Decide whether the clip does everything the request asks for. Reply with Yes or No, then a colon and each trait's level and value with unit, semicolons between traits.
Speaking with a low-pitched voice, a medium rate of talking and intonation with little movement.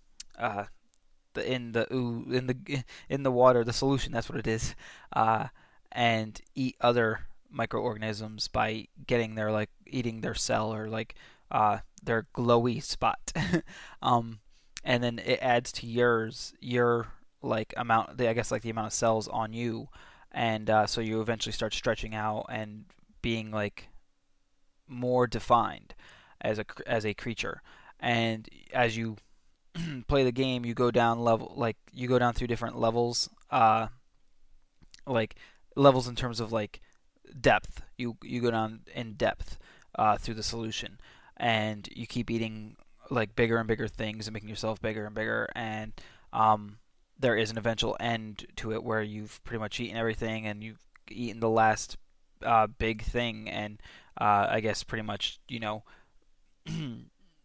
Yes: low, 115 Hz; average, 160 wpm; narrow, 1.8 semitones